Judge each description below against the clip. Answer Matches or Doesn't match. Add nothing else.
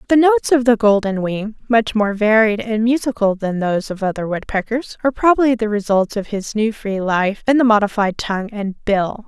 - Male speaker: Doesn't match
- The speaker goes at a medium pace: Matches